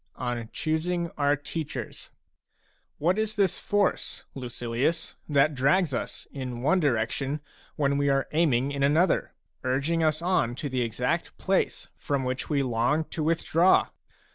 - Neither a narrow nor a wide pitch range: Yes, average, 4.2 semitones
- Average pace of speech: Yes, average, 150 wpm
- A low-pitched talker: No, medium, 145 Hz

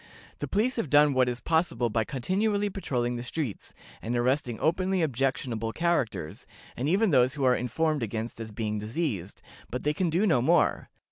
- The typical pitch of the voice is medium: No, low, 130 Hz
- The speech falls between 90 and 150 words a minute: No, average, 180 wpm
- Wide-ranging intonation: Yes, wide, 5.8 semitones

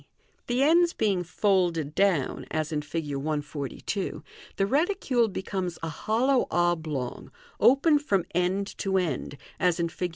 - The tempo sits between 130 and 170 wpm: Yes, average, 140 wpm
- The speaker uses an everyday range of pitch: No, wide, 5.7 semitones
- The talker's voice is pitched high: No, medium, 180 Hz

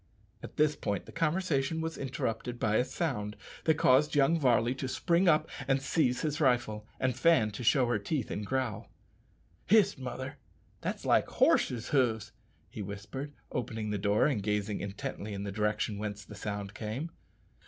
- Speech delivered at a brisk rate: No, average, 170 wpm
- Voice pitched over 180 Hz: No, low, 125 Hz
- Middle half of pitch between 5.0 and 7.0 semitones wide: Yes, wide, 5.6 semitones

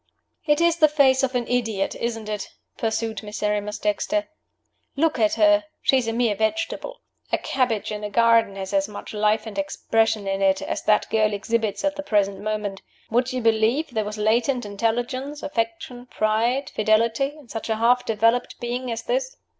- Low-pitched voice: No, high, 225 Hz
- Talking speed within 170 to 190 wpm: Yes, average, 180 wpm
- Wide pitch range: No, average, 3.4 semitones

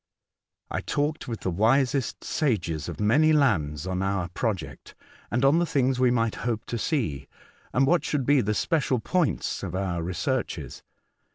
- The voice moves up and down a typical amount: No, wide, 6.7 semitones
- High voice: No, low, 120 Hz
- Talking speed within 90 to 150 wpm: No, average, 165 wpm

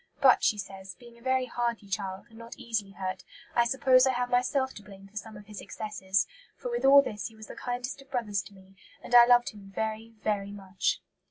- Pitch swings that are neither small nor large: Yes, average, 3.7 semitones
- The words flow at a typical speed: No, fast, 230 wpm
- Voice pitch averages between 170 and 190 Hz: No, high, 220 Hz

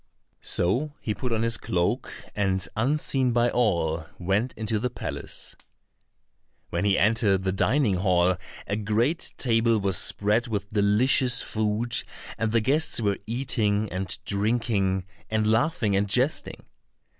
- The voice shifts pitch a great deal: No, average, 3.4 semitones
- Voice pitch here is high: No, low, 110 Hz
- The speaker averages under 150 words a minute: Yes, slow, 135 wpm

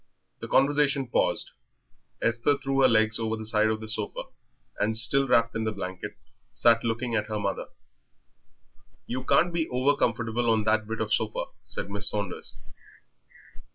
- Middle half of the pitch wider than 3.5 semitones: No, average, 2.9 semitones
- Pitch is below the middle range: Yes, low, 115 Hz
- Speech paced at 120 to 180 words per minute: Yes, average, 160 wpm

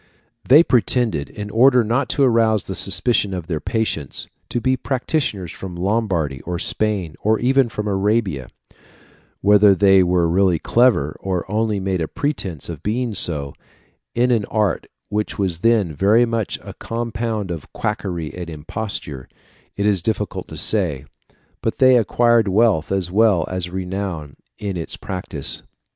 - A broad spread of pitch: No, average, 4.4 semitones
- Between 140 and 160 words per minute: Yes, average, 155 wpm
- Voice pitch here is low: Yes, low, 100 Hz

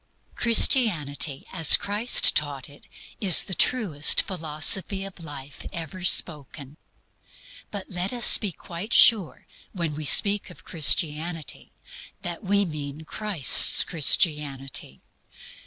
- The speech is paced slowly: Yes, slow, 105 wpm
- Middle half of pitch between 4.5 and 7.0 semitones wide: Yes, average, 4.8 semitones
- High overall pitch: No, medium, 165 Hz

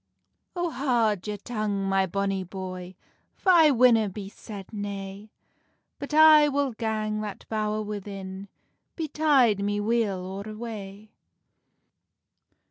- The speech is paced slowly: Yes, slow, 120 wpm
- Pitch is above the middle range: Yes, high, 210 Hz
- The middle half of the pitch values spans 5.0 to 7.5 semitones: No, average, 3.4 semitones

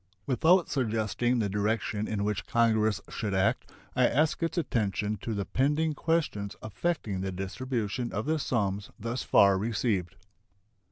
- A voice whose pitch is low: Yes, low, 110 Hz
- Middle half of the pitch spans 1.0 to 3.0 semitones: No, average, 4.3 semitones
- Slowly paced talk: No, average, 145 wpm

